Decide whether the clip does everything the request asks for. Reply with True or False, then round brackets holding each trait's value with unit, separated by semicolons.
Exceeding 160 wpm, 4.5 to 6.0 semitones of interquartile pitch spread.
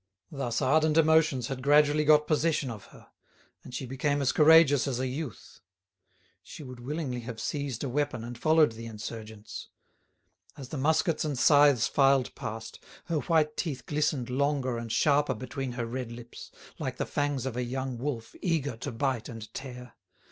False (170 wpm; 3.5 semitones)